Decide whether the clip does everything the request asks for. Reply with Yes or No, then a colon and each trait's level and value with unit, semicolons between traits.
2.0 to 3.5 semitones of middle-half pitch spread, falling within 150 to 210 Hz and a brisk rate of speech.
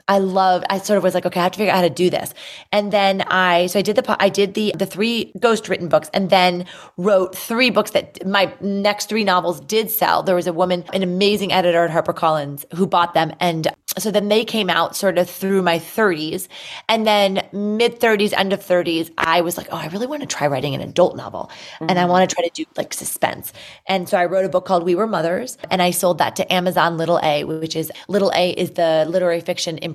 Yes: narrow, 2.6 semitones; medium, 185 Hz; fast, 245 wpm